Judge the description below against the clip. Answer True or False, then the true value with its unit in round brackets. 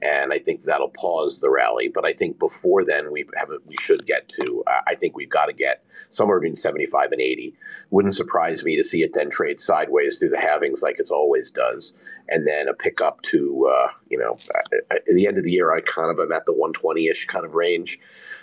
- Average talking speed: False (230 wpm)